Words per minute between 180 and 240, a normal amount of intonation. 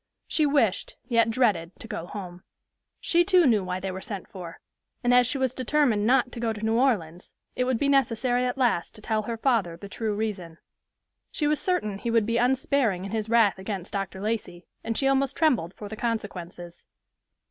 Yes: average, 200 wpm; average, 4.6 semitones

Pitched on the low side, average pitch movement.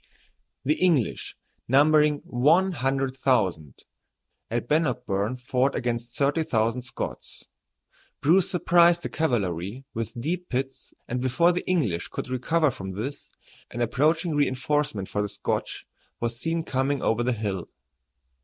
Yes: low, 130 Hz; average, 4.8 semitones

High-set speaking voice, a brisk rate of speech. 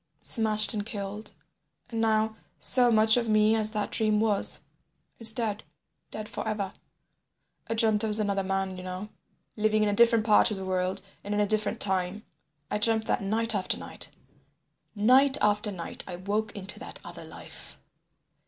No: high, 215 Hz; average, 170 wpm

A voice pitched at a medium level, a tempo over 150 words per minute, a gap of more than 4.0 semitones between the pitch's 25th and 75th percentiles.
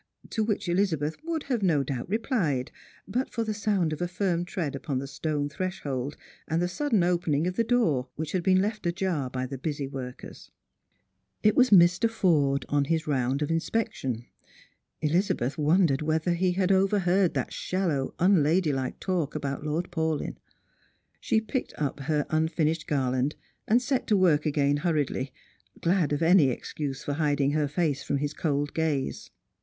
Yes: medium, 160 Hz; average, 170 wpm; average, 4.6 semitones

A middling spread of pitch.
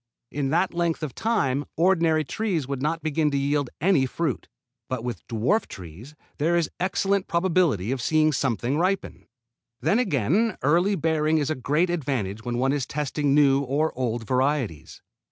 Yes: average, 4.5 semitones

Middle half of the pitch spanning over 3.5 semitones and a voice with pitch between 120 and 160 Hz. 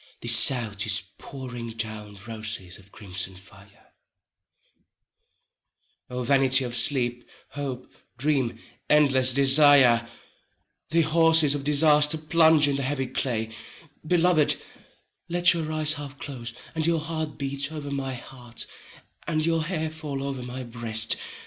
Yes: average, 4.5 semitones; low, 135 Hz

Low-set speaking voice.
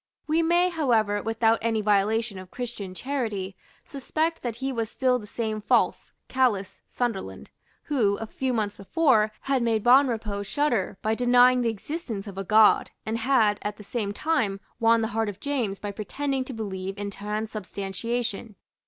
No: high, 225 Hz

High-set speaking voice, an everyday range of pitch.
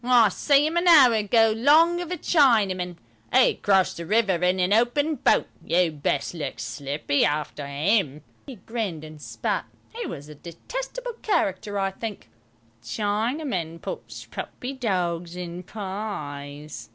No: high, 195 Hz; wide, 7.1 semitones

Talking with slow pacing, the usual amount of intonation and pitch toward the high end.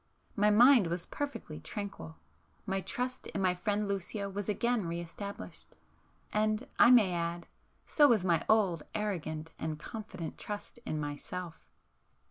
Yes: slow, 130 wpm; average, 4.1 semitones; high, 195 Hz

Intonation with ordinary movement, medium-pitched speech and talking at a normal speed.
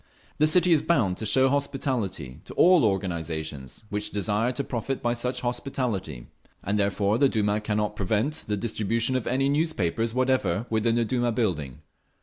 No: average, 4.5 semitones; low, 110 Hz; average, 160 wpm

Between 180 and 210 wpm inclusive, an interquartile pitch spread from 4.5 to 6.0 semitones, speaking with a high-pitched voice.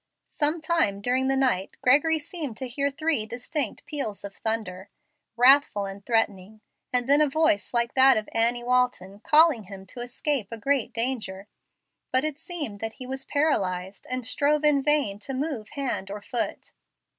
No: average, 170 wpm; average, 5.2 semitones; very high, 250 Hz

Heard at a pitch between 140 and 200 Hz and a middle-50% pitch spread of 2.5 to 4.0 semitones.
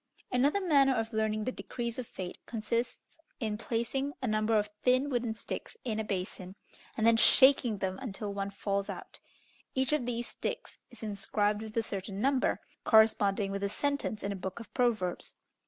No: high, 220 Hz; average, 3.5 semitones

